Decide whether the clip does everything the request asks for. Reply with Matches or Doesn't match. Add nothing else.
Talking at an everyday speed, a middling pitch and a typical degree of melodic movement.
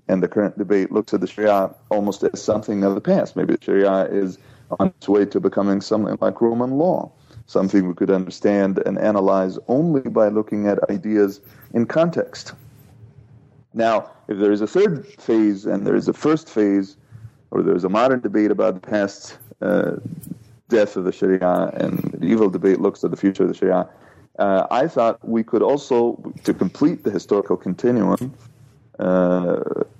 Doesn't match